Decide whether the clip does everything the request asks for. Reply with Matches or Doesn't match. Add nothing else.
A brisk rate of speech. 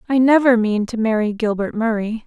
Doesn't match